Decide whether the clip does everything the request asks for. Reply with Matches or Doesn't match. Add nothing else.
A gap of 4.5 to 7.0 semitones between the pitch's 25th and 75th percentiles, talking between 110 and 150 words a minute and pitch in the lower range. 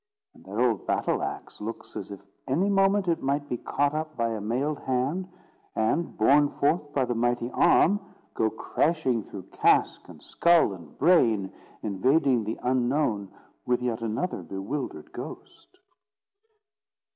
Matches